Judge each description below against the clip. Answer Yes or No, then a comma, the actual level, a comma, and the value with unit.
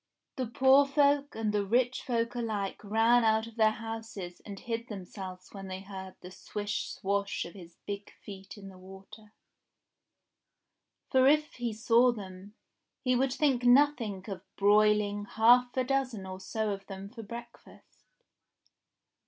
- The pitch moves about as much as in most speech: Yes, average, 3.7 semitones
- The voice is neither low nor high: No, high, 215 Hz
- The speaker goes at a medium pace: Yes, average, 155 wpm